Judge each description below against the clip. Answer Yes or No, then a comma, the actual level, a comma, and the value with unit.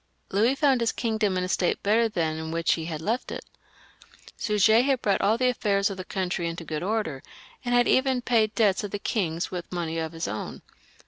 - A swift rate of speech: Yes, fast, 220 wpm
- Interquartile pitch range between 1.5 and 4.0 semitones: No, wide, 5.4 semitones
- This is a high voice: Yes, high, 200 Hz